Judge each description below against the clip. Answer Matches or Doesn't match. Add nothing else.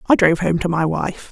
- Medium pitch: Matches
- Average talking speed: Doesn't match